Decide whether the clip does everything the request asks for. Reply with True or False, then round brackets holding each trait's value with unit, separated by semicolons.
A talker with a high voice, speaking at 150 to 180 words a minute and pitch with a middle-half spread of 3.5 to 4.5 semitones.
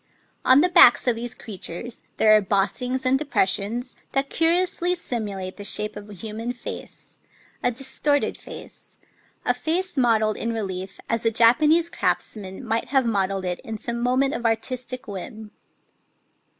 True (230 Hz; 165 wpm; 3.9 semitones)